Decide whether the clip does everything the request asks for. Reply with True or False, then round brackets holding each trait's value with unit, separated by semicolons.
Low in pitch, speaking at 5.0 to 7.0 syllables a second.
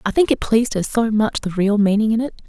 False (215 Hz; 6.2 syllables/s)